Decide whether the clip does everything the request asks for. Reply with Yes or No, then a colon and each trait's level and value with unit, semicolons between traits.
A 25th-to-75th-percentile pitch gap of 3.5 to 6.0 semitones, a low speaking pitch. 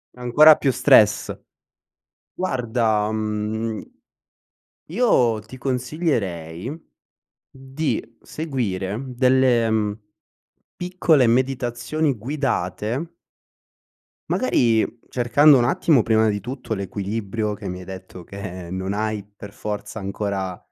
Yes: average, 4.3 semitones; low, 115 Hz